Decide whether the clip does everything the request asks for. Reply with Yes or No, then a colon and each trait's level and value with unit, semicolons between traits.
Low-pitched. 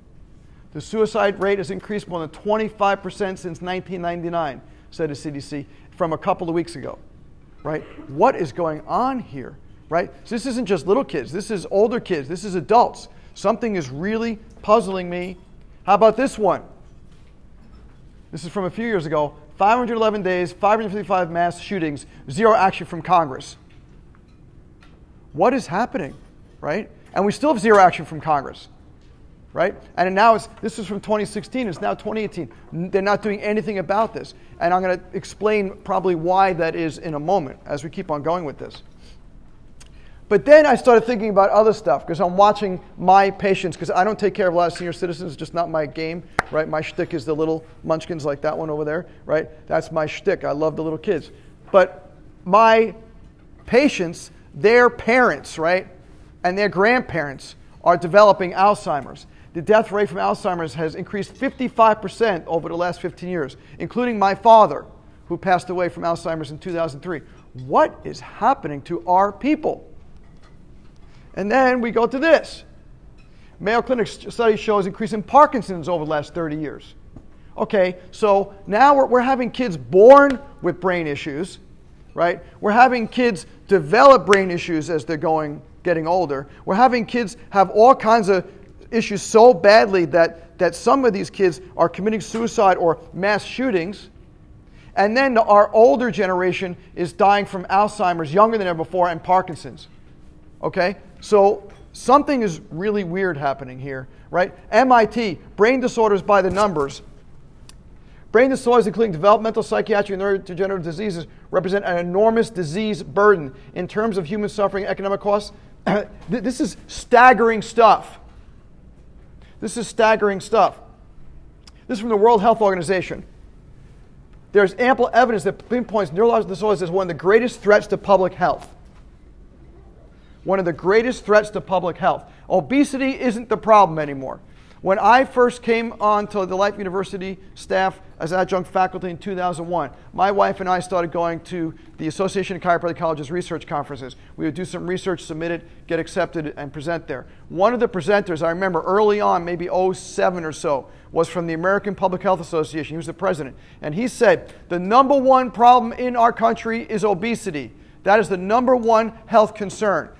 No: high, 190 Hz